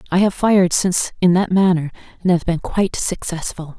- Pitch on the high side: No, medium, 180 Hz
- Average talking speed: Yes, average, 190 wpm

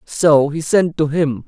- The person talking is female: No, male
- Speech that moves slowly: No, fast, 205 wpm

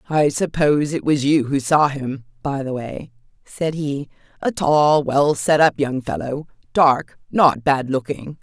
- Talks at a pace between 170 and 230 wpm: No, average, 150 wpm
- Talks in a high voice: No, medium, 140 Hz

